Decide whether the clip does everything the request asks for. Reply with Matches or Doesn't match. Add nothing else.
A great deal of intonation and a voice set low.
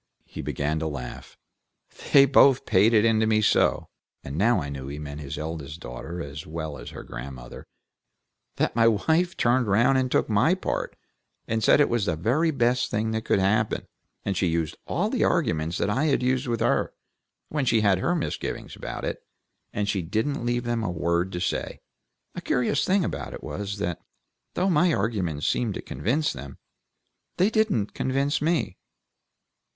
Matches